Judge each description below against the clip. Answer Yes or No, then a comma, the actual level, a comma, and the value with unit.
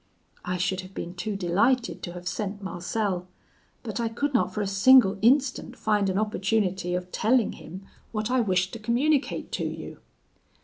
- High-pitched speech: Yes, high, 200 Hz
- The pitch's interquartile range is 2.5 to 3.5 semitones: No, average, 4.0 semitones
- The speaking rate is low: No, average, 175 wpm